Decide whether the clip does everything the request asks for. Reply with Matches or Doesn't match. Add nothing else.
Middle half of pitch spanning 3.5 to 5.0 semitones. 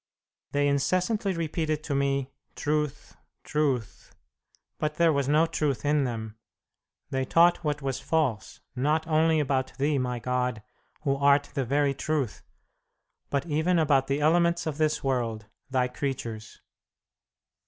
Doesn't match